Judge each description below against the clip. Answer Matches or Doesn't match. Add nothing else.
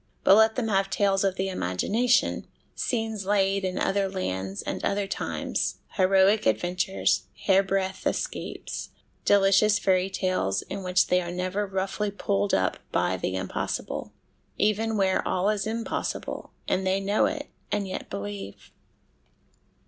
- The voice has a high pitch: Matches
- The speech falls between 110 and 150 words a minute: Matches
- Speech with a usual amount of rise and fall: Doesn't match